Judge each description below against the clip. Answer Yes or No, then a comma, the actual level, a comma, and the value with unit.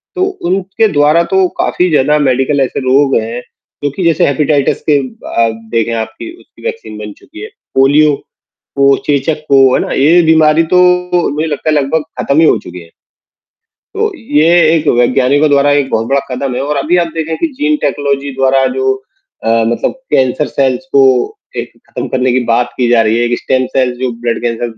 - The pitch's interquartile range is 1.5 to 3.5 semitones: No, average, 3.9 semitones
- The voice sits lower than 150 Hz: Yes, medium, 140 Hz